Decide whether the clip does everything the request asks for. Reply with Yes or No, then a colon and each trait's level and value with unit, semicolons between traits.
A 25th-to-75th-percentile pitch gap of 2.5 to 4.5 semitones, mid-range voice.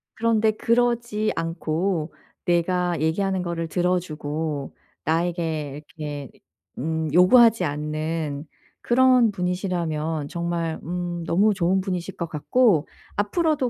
Yes: average, 3.9 semitones; medium, 175 Hz